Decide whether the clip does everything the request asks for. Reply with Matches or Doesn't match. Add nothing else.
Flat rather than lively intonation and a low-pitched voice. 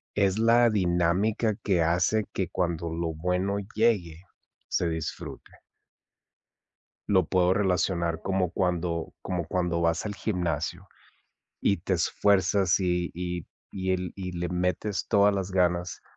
Matches